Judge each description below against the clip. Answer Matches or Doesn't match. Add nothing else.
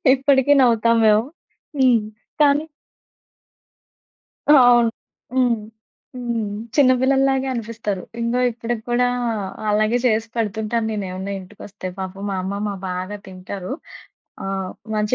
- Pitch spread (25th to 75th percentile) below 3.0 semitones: Doesn't match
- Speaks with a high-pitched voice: Matches